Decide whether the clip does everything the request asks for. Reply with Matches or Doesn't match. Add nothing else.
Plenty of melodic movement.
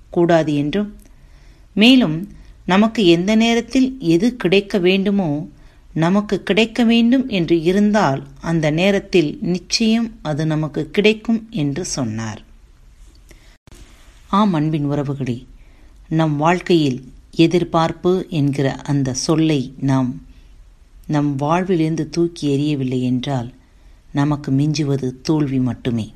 Matches